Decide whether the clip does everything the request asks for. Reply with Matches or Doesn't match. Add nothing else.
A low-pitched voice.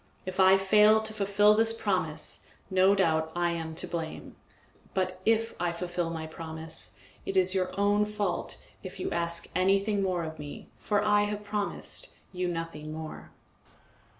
Doesn't match